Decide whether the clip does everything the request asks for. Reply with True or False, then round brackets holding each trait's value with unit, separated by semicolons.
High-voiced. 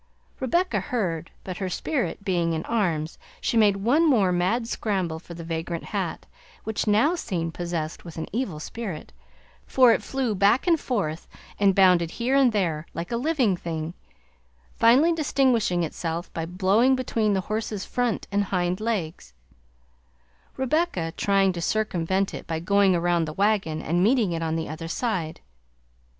True (195 Hz)